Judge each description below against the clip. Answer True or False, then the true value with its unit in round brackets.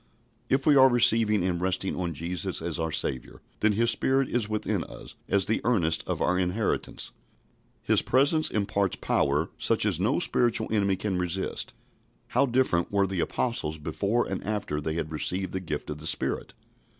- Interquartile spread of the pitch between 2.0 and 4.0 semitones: False (4.9 semitones)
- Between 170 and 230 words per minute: True (175 wpm)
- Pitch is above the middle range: False (95 Hz)